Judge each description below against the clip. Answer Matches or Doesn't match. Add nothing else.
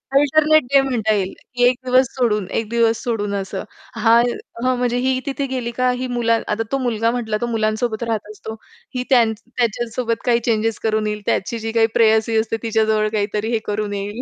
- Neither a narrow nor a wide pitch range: Doesn't match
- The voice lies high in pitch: Matches